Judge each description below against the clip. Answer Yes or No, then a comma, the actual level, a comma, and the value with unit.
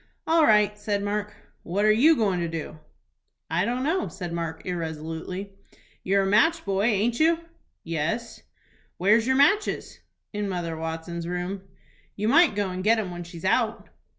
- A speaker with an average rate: Yes, average, 165 wpm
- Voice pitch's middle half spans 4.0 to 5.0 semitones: Yes, average, 4.7 semitones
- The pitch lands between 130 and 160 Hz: No, high, 200 Hz